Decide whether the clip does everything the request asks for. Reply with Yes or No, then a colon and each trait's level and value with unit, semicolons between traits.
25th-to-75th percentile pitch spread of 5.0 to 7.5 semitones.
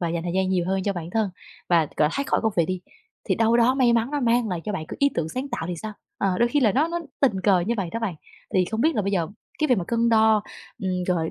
No: average, 4.6 semitones